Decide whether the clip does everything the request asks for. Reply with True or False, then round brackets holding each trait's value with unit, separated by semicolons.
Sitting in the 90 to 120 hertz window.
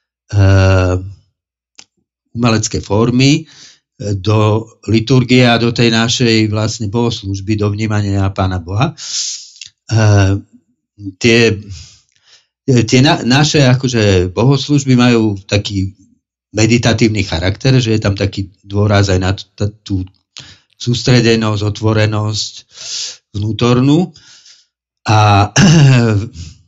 True (110 Hz)